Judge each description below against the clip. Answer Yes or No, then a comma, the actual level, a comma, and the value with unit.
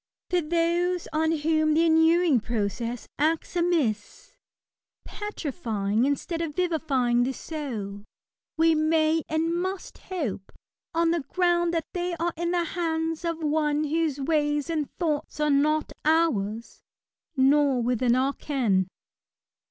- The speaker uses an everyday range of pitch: Yes, average, 3.9 semitones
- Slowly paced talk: Yes, slow, 130 wpm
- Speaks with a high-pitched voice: Yes, very high, 310 Hz